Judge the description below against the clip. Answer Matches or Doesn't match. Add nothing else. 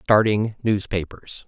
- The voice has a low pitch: Matches